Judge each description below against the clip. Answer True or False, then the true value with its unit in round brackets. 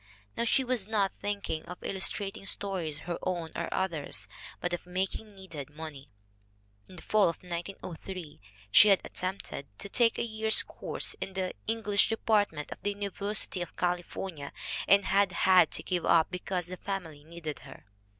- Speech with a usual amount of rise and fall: True (3.1 semitones)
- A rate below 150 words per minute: False (180 wpm)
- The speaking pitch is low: False (185 Hz)